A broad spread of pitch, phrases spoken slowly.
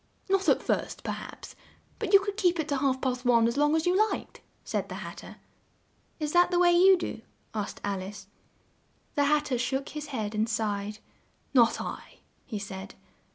No: wide, 7.9 semitones; average, 200 wpm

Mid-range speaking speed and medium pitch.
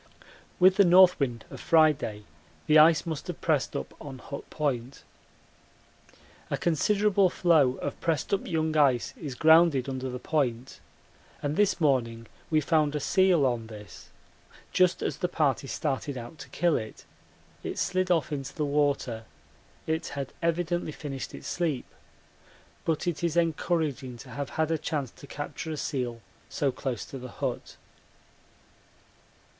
Yes: average, 155 wpm; medium, 150 Hz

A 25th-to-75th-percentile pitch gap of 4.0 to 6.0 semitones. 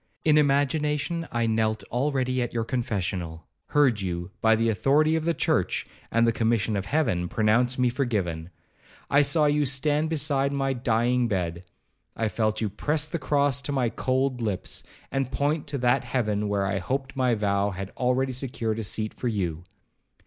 Yes: average, 4.7 semitones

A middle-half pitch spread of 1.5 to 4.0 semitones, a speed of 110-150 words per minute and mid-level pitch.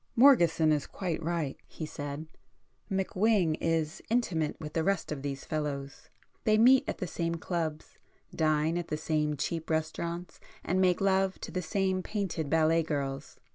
Yes: average, 3.4 semitones; average, 145 wpm; medium, 165 Hz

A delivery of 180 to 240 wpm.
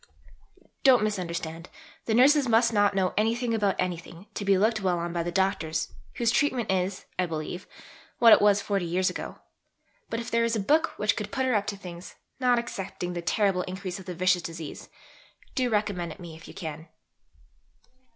Yes: average, 190 wpm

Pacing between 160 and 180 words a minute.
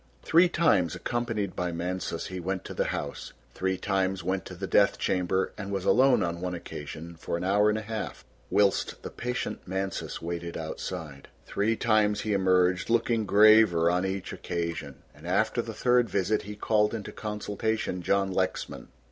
Yes: average, 175 wpm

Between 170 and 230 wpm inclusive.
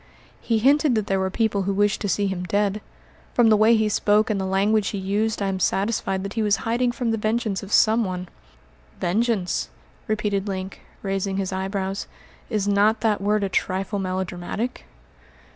Yes: average, 185 wpm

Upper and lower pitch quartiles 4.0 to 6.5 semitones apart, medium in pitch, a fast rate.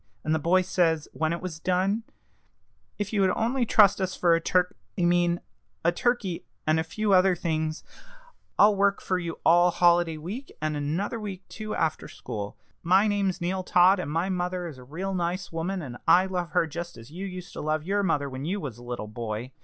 No: average, 3.3 semitones; medium, 175 Hz; fast, 210 wpm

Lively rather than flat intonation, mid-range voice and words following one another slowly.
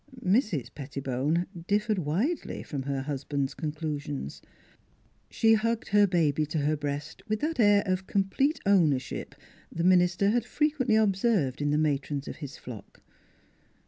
No: wide, 6.4 semitones; medium, 170 Hz; average, 145 wpm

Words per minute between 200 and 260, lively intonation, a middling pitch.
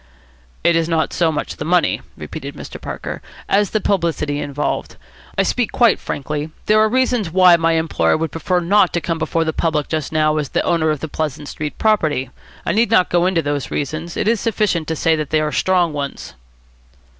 No: fast, 205 wpm; average, 3.3 semitones; medium, 165 Hz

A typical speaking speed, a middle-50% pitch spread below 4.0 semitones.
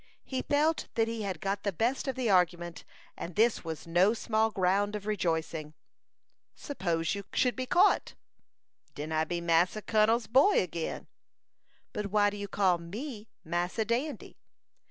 No: average, 155 wpm; average, 4.9 semitones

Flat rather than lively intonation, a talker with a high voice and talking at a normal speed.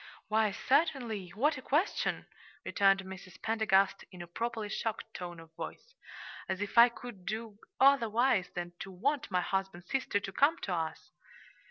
No: average, 4.3 semitones; high, 205 Hz; average, 160 wpm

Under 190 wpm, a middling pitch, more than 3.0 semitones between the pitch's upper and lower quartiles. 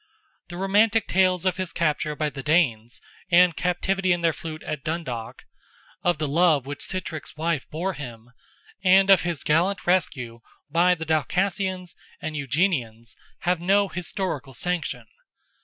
Yes: average, 145 wpm; medium, 170 Hz; average, 3.9 semitones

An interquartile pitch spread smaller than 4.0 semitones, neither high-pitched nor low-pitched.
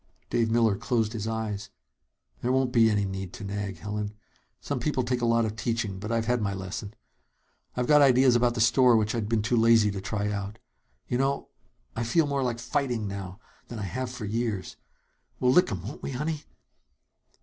No: average, 3.1 semitones; low, 115 Hz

